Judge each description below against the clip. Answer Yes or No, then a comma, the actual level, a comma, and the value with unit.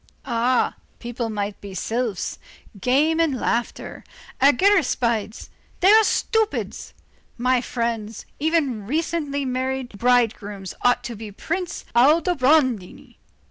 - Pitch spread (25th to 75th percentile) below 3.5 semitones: No, average, 5.3 semitones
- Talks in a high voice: Yes, very high, 250 Hz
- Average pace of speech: No, slow, 100 wpm